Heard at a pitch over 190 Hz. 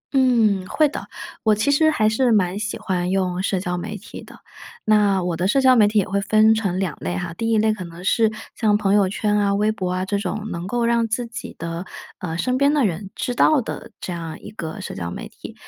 Yes: high, 205 Hz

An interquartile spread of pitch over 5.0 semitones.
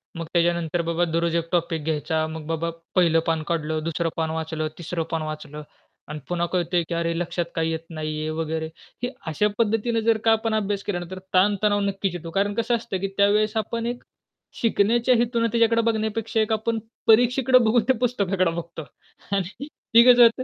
Yes: wide, 5.4 semitones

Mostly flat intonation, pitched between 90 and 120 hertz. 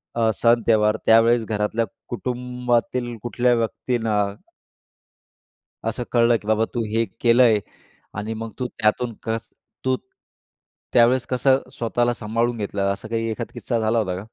Yes: narrow, 1.7 semitones; low, 115 Hz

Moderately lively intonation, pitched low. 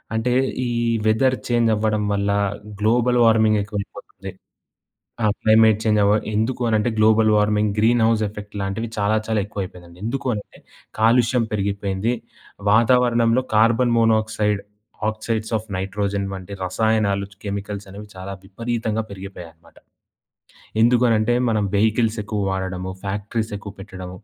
No: narrow, 2.1 semitones; low, 110 Hz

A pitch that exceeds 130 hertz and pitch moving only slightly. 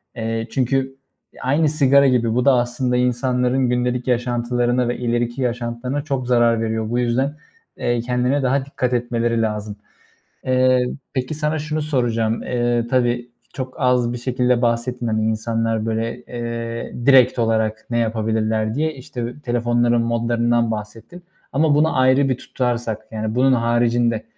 No: low, 120 Hz; narrow, 1.7 semitones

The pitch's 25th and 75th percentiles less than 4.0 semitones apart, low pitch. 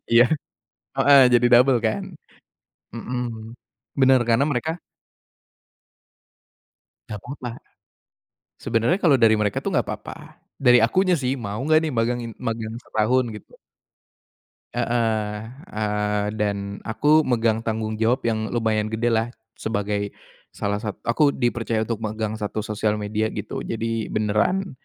Yes: narrow, 2.4 semitones; low, 115 Hz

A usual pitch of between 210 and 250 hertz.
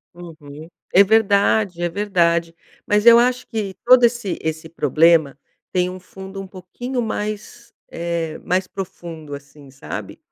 No: medium, 185 Hz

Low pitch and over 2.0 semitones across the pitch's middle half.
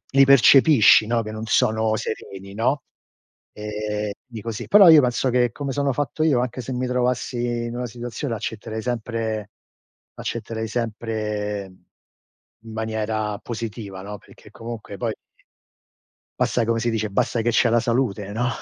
Yes: low, 115 Hz; narrow, 2.4 semitones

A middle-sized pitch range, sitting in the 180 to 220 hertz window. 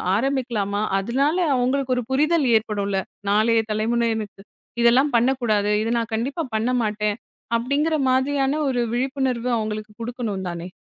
No: average, 3.7 semitones; high, 235 Hz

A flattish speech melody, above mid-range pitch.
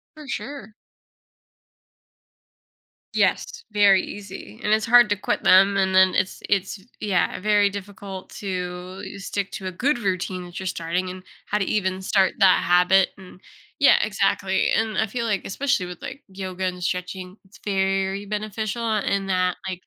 Yes: narrow, 2.0 semitones; high, 195 Hz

